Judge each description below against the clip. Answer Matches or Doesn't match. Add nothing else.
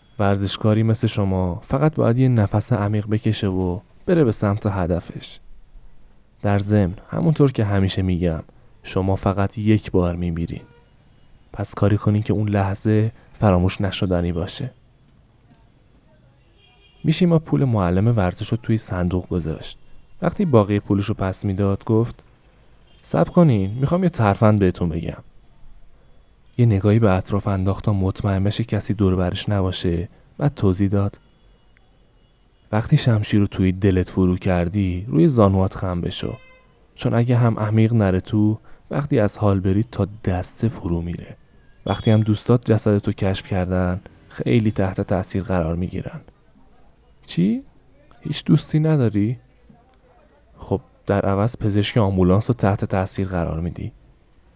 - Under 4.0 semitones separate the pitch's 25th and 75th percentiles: Matches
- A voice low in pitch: Matches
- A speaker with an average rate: Matches